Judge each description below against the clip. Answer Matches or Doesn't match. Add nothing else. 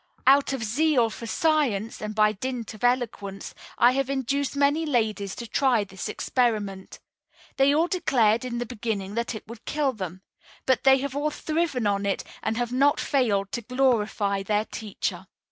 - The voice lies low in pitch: Doesn't match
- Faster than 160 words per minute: Matches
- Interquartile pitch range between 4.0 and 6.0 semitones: Matches